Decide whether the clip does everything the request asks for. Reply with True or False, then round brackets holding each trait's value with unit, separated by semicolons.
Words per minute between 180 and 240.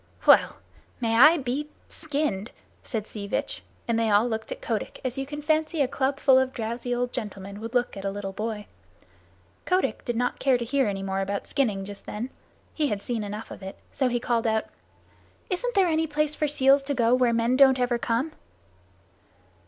True (200 wpm)